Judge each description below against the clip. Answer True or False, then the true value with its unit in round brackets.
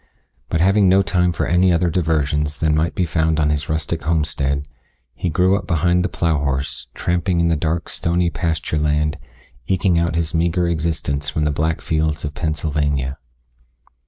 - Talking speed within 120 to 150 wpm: False (175 wpm)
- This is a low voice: True (80 Hz)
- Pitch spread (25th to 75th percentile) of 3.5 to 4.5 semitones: False (2.5 semitones)